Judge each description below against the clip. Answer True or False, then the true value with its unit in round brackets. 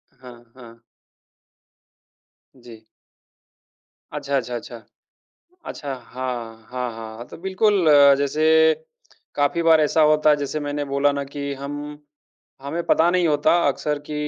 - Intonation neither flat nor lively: True (3.5 semitones)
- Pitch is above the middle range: False (140 Hz)